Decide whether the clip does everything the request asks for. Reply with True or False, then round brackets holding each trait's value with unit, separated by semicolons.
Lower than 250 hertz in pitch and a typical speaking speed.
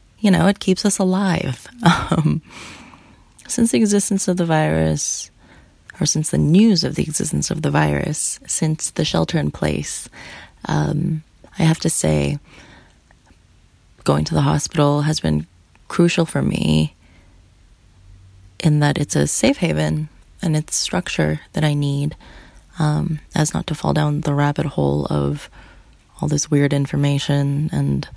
True (140 Hz; 145 wpm)